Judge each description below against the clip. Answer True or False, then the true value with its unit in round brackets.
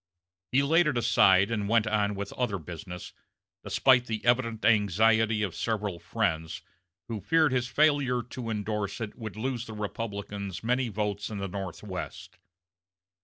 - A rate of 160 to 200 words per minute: False (150 wpm)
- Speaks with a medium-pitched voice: False (110 Hz)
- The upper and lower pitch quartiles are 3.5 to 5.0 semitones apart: False (3.1 semitones)